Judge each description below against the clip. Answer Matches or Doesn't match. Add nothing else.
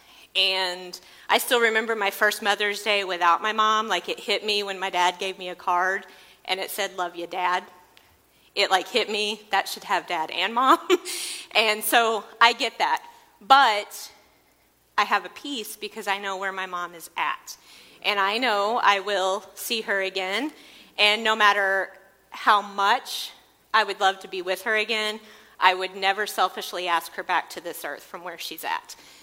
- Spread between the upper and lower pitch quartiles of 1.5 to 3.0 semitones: Matches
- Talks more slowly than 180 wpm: Doesn't match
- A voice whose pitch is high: Matches